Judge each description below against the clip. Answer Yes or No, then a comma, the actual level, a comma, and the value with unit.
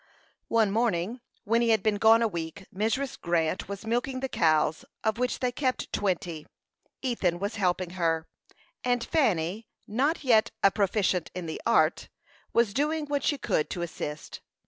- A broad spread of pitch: Yes, wide, 5.7 semitones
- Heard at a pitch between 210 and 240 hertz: Yes, high, 215 Hz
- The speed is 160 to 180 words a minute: Yes, average, 165 wpm